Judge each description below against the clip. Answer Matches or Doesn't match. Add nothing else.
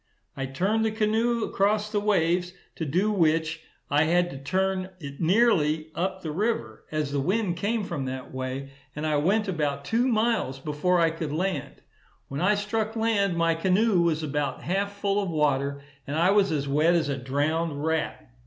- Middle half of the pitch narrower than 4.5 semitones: Doesn't match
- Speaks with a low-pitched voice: Doesn't match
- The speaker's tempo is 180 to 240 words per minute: Matches